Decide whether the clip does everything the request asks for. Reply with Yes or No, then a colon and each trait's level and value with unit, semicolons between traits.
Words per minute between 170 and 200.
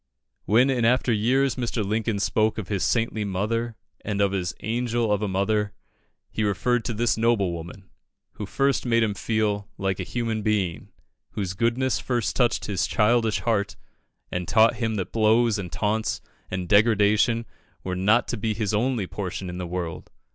Yes: average, 175 wpm